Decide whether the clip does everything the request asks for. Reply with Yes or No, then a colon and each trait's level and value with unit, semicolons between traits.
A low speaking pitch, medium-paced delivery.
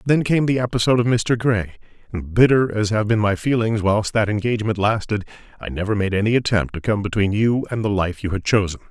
No: low, 110 Hz; fast, 220 wpm